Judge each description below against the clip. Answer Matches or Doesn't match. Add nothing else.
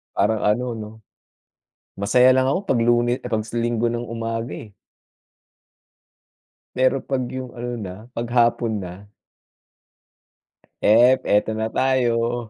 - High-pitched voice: Doesn't match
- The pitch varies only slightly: Matches